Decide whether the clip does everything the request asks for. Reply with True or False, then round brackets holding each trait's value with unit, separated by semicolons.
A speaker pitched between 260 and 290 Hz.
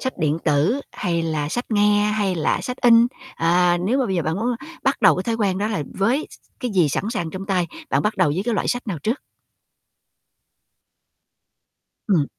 False (195 Hz)